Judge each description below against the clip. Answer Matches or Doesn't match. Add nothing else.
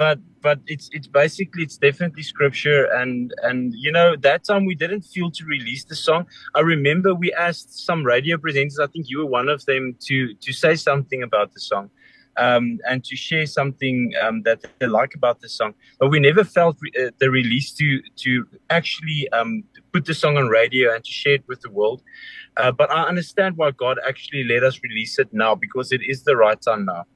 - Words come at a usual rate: Doesn't match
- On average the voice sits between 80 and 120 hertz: Doesn't match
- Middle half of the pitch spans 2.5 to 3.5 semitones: Doesn't match